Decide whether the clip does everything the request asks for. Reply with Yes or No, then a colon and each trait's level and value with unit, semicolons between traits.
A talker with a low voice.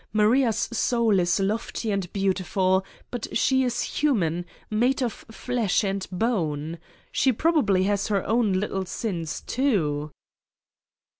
No: high, 205 Hz